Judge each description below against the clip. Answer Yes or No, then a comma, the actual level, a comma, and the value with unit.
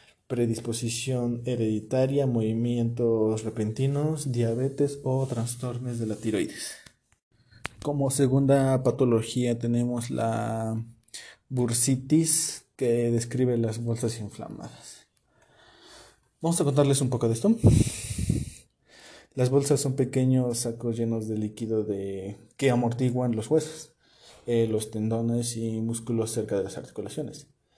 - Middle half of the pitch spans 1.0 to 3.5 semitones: Yes, narrow, 2.6 semitones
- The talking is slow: Yes, slow, 110 wpm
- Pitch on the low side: Yes, low, 120 Hz